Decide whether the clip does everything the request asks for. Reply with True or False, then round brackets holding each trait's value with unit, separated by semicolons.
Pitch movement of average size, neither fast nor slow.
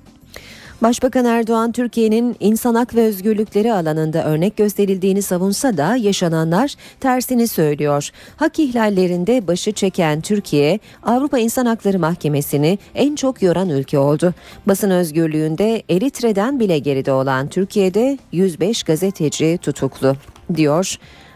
False (6.6 semitones; 110 wpm)